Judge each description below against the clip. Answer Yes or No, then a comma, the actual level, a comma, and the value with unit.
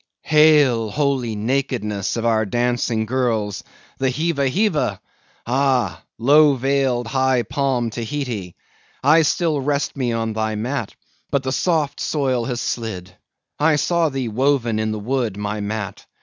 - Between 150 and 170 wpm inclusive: No, slow, 135 wpm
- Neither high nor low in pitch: No, low, 125 Hz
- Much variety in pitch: No, average, 4.0 semitones